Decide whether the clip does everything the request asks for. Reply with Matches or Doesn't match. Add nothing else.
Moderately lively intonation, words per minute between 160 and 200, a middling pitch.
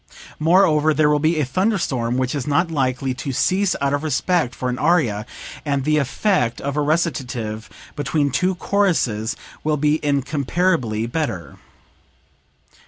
Doesn't match